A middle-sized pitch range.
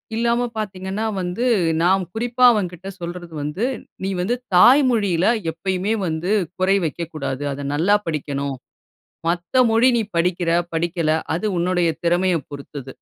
Yes: average, 3.6 semitones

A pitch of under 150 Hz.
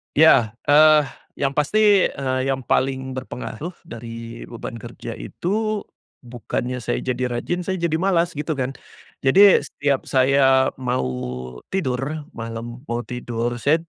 Yes: low, 135 Hz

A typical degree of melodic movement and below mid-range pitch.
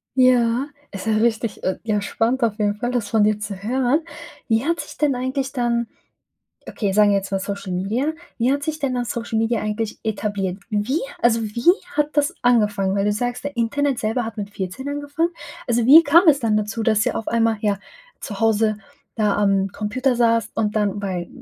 No: average, 3.5 semitones; high, 225 Hz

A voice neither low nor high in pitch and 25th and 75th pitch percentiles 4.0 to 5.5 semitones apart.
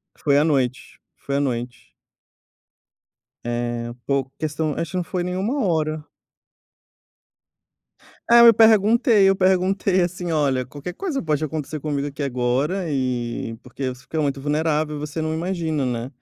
Yes: medium, 150 Hz; average, 5.1 semitones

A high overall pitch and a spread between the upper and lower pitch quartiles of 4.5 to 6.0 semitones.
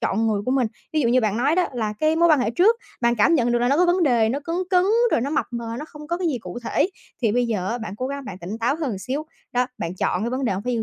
Yes: high, 245 Hz; average, 5.1 semitones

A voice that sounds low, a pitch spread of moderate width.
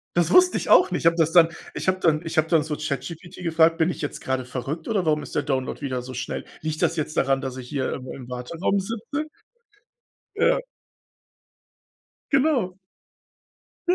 No: medium, 160 Hz; average, 4.9 semitones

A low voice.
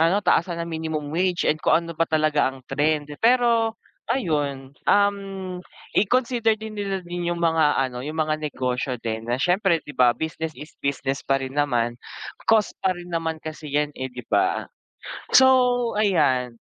No: medium, 160 Hz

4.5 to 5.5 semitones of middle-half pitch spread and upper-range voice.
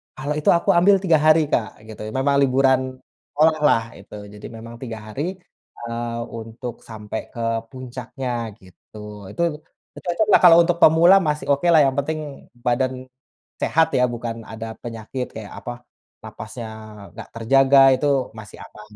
No: average, 5.0 semitones; low, 130 Hz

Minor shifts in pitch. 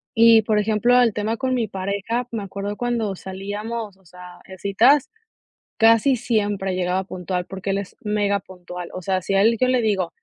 No: average, 3.2 semitones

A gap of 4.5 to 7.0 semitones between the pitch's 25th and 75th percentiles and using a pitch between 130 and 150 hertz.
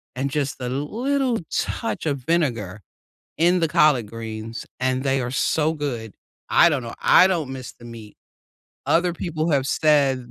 Yes: average, 5.0 semitones; medium, 140 Hz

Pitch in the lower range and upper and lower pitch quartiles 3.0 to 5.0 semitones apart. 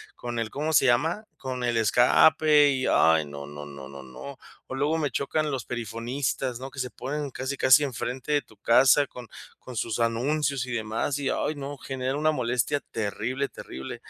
Yes: low, 130 Hz; average, 3.6 semitones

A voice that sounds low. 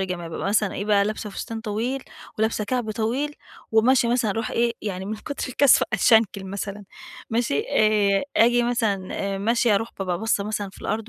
No: high, 215 Hz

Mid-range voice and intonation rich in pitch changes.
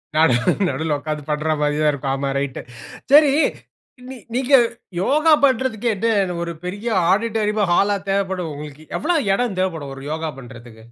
Yes: medium, 180 Hz; wide, 7.1 semitones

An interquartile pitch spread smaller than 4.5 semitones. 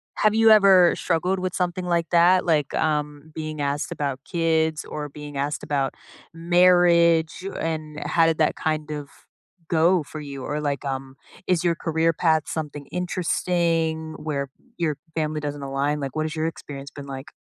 Yes: narrow, 2.6 semitones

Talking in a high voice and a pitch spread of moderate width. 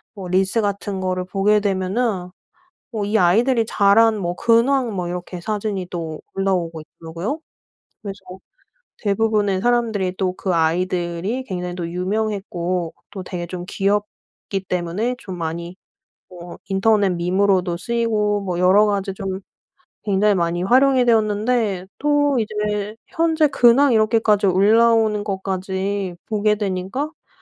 Yes: high, 200 Hz; average, 3.2 semitones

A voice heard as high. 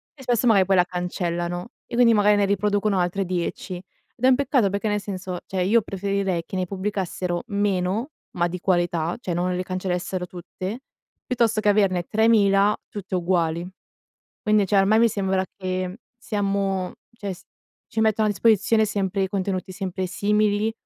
Yes: high, 195 Hz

